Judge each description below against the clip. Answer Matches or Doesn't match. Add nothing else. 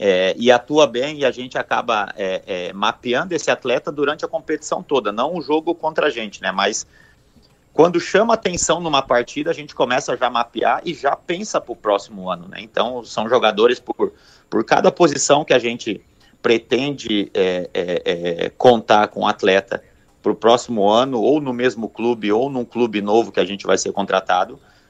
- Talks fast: Matches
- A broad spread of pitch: Matches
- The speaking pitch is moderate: Matches